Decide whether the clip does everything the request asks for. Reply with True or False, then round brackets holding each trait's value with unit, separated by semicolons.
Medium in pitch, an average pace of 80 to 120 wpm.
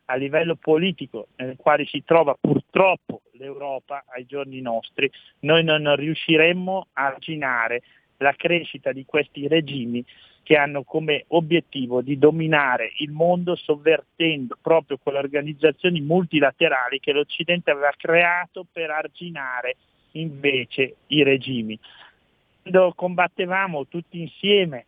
True (155 Hz; 115 wpm)